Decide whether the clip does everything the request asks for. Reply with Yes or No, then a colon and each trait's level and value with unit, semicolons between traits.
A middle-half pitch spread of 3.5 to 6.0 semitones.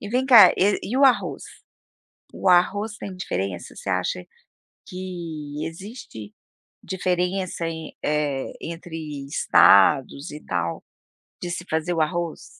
Yes: average, 4.6 semitones